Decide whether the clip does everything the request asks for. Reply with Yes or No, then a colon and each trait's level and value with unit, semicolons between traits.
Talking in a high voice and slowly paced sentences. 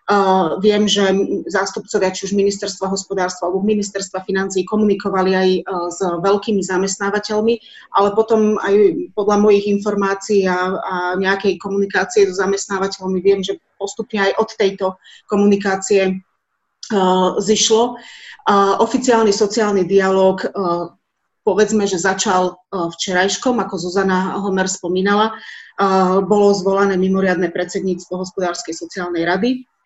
Yes: high, 195 Hz; slow, 105 wpm